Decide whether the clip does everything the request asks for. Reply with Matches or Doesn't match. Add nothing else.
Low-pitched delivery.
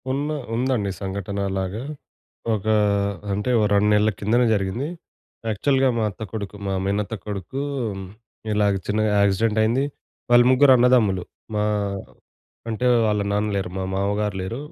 Matches